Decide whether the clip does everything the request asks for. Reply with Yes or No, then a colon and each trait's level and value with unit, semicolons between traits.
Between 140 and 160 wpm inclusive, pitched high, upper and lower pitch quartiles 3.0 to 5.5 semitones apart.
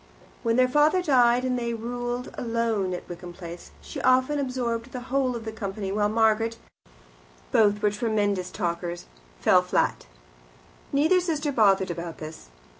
Yes: average, 150 wpm; high, 230 Hz; average, 4.4 semitones